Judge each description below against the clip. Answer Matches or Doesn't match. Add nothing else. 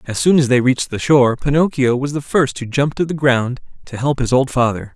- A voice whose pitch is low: Matches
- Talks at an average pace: Doesn't match